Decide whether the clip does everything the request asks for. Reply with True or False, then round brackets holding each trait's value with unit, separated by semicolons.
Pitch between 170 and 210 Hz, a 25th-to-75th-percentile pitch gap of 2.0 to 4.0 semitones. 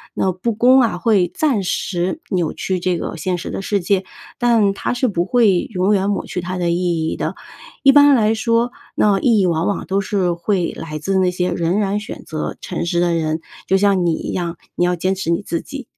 True (190 Hz; 3.3 semitones)